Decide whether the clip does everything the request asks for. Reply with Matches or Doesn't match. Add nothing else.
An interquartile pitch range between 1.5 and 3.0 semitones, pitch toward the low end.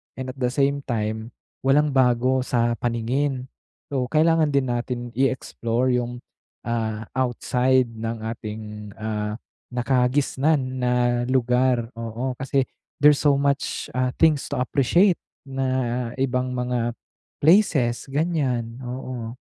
Matches